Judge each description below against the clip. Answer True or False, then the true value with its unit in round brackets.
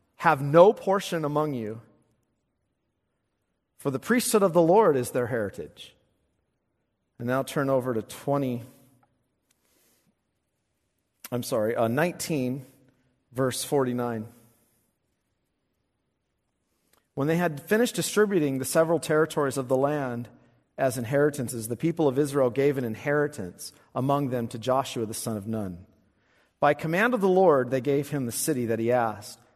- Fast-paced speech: False (140 wpm)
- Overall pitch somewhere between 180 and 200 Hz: False (130 Hz)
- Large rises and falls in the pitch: False (4.0 semitones)